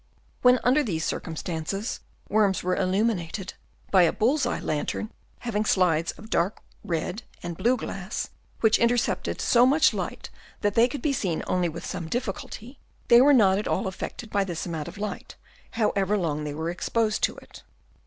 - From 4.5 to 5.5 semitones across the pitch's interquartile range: Yes, average, 5.1 semitones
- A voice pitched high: Yes, high, 200 Hz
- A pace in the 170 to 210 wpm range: Yes, average, 175 wpm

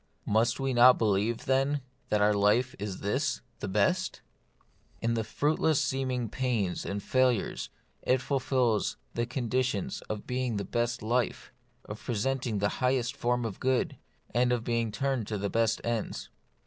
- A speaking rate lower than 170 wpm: Yes, average, 155 wpm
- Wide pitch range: No, average, 3.3 semitones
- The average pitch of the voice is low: Yes, low, 120 Hz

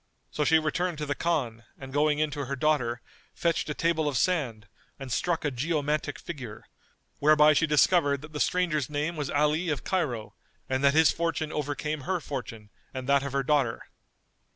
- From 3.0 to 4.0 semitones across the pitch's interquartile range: No, narrow, 2.6 semitones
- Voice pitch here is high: No, medium, 150 Hz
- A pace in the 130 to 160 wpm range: No, average, 185 wpm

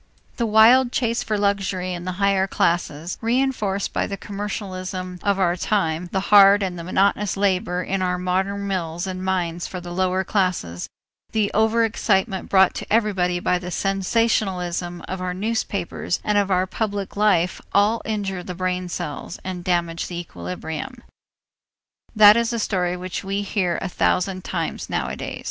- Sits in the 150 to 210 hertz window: Yes, high, 190 Hz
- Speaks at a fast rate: No, average, 160 wpm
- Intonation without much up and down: Yes, narrow, 2.3 semitones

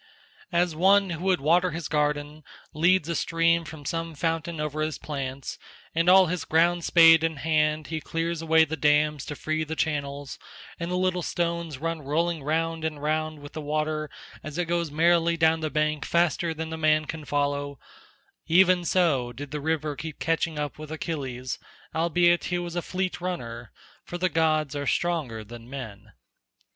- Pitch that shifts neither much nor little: No, narrow, 2.3 semitones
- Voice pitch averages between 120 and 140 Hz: No, medium, 160 Hz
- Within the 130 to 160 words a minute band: No, average, 175 wpm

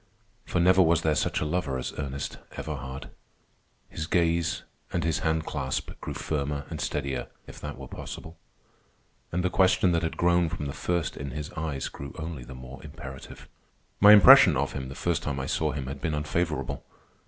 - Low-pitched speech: Yes, very low, 75 Hz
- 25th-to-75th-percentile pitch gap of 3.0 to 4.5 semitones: Yes, average, 3.8 semitones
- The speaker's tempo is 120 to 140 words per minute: No, average, 190 wpm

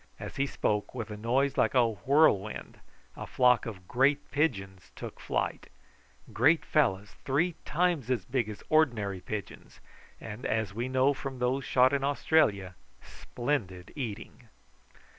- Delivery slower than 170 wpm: Yes, average, 140 wpm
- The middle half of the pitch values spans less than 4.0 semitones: No, average, 5.0 semitones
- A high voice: No, low, 125 Hz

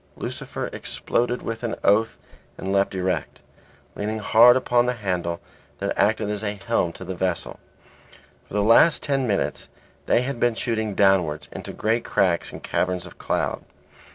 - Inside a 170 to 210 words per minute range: No, average, 160 wpm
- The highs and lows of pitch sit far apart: No, average, 3.7 semitones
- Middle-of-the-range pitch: No, low, 105 Hz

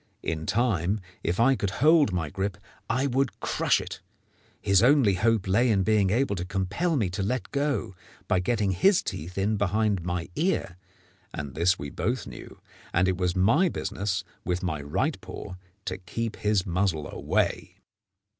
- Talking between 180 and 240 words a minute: No, average, 170 wpm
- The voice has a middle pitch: No, low, 100 Hz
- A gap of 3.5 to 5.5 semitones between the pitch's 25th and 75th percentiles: Yes, average, 4.5 semitones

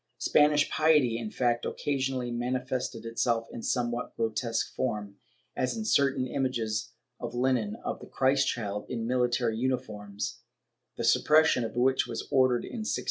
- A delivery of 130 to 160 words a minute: Yes, average, 150 wpm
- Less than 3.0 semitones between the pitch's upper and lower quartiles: Yes, narrow, 2.4 semitones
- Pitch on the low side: Yes, low, 125 Hz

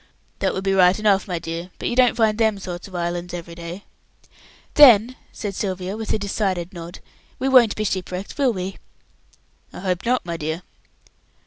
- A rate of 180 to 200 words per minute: Yes, average, 190 wpm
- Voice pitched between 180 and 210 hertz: Yes, high, 190 Hz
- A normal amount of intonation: Yes, average, 3.6 semitones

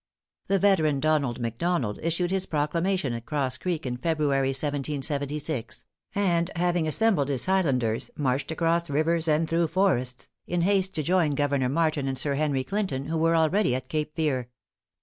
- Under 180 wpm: Yes, average, 160 wpm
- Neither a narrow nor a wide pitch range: Yes, average, 3.9 semitones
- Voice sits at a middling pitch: Yes, medium, 155 Hz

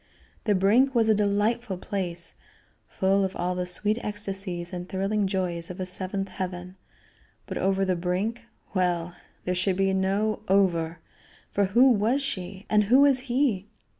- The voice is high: Yes, high, 195 Hz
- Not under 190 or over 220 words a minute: No, average, 160 wpm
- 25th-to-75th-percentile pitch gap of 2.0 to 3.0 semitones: Yes, narrow, 2.6 semitones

